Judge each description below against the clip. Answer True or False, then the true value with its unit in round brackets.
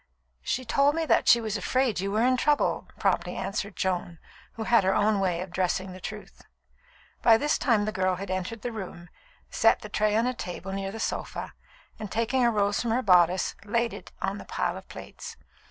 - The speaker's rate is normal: False (210 wpm)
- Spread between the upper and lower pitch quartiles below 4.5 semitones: True (3.9 semitones)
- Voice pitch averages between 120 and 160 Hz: False (210 Hz)